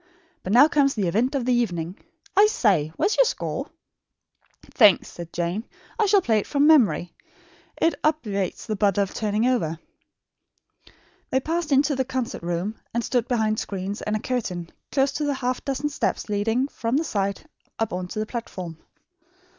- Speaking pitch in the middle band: No, high, 225 Hz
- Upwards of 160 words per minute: Yes, average, 180 wpm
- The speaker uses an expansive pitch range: Yes, wide, 5.7 semitones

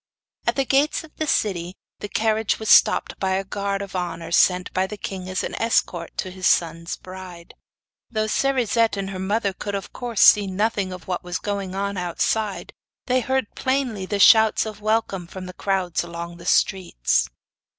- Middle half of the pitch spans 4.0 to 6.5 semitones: No, average, 3.0 semitones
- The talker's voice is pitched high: Yes, high, 195 Hz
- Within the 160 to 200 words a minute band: Yes, average, 185 wpm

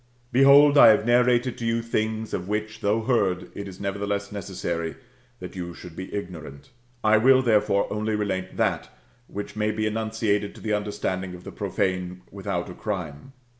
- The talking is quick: No, average, 175 wpm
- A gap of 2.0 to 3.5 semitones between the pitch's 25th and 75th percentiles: Yes, average, 3.0 semitones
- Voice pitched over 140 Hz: No, low, 105 Hz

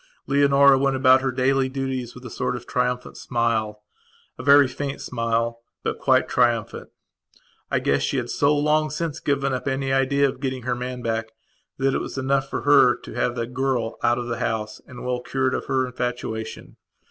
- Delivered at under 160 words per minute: No, average, 195 wpm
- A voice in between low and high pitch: No, low, 130 Hz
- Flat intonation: Yes, narrow, 2.1 semitones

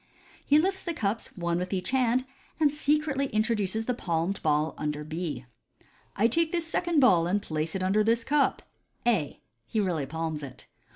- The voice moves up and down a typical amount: No, wide, 8.6 semitones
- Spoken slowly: No, average, 185 wpm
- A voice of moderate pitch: No, high, 210 Hz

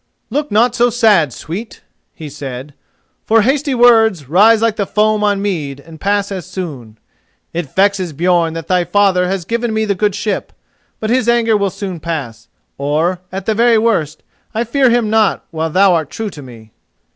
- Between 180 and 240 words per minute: Yes, average, 185 wpm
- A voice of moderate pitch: No, high, 195 Hz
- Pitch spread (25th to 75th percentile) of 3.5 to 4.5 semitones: No, average, 5.3 semitones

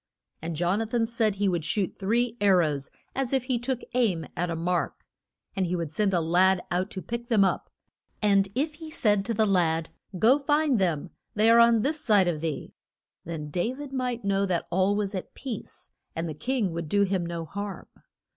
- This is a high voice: Yes, high, 200 Hz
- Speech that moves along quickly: Yes, fast, 210 wpm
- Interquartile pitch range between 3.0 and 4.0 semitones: No, average, 5.1 semitones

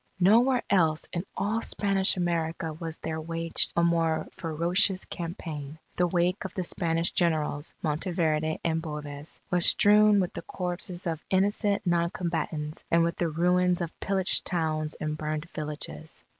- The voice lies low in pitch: No, medium, 170 Hz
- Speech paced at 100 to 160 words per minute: Yes, average, 150 wpm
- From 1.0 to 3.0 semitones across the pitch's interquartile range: Yes, narrow, 2.4 semitones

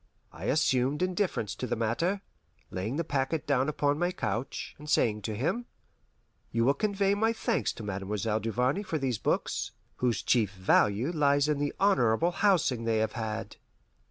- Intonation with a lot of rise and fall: Yes, wide, 6.9 semitones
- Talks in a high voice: No, low, 135 Hz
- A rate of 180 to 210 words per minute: No, average, 165 wpm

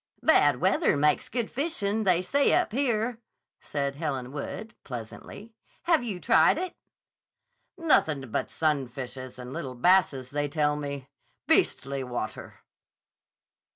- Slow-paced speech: Yes, slow, 120 wpm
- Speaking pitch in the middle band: Yes, medium, 150 Hz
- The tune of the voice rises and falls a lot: Yes, wide, 8.6 semitones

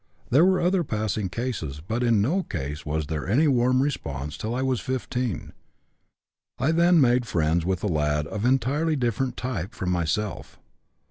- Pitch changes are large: Yes, wide, 7.3 semitones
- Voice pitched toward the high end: No, low, 115 Hz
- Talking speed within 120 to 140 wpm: No, average, 170 wpm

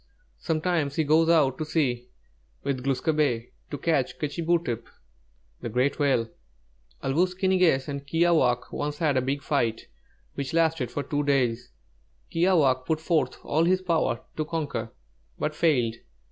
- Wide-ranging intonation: No, average, 3.8 semitones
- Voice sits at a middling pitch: Yes, medium, 145 Hz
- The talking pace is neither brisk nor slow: Yes, average, 160 wpm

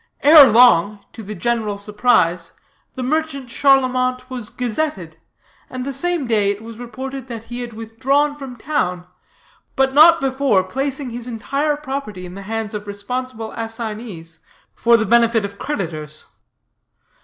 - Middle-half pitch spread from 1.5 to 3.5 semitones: No, average, 4.2 semitones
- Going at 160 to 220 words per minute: No, average, 145 wpm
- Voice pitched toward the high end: Yes, high, 235 Hz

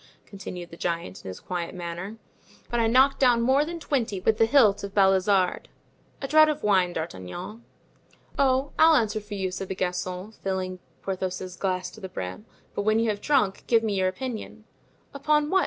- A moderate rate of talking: Yes, average, 190 wpm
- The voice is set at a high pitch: Yes, high, 205 Hz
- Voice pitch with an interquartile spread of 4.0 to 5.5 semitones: Yes, average, 5.0 semitones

